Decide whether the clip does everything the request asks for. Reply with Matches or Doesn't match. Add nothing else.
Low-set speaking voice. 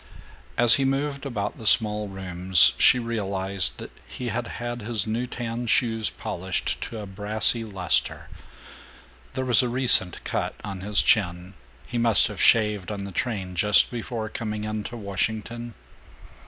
Matches